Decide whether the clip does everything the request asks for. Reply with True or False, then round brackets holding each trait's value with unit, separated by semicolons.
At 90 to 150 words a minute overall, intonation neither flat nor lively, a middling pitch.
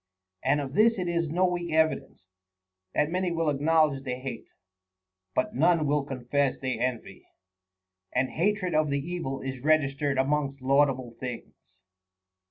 True (145 wpm; 3.6 semitones; 145 Hz)